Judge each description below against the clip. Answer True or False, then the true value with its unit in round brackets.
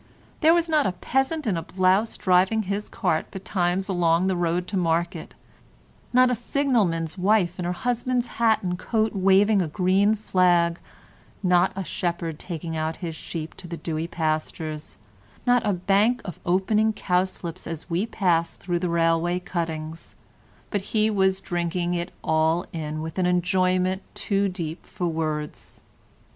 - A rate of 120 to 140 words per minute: False (155 wpm)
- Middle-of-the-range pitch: True (180 Hz)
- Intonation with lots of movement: False (3.2 semitones)